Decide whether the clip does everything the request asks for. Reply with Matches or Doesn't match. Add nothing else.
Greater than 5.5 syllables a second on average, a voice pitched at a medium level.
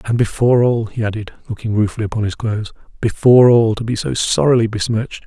Doesn't match